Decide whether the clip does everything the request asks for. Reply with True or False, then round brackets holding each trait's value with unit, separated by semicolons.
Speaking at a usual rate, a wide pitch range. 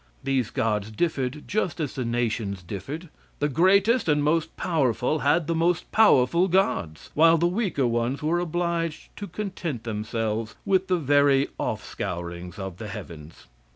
True (155 wpm; 7.3 semitones)